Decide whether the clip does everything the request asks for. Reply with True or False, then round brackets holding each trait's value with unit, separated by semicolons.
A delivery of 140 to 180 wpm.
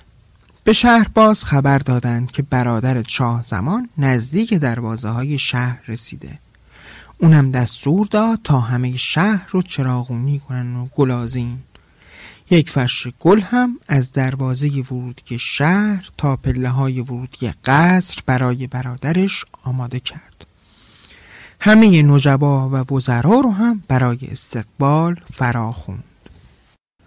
False (115 wpm)